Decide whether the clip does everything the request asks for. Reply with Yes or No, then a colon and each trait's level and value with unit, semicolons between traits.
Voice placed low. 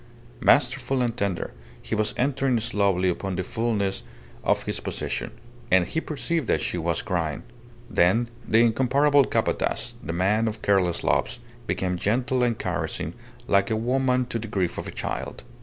Yes: low, 110 Hz